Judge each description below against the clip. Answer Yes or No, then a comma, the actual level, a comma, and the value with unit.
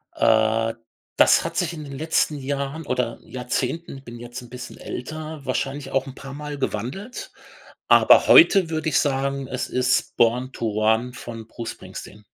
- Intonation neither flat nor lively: Yes, average, 3.7 semitones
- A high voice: No, low, 130 Hz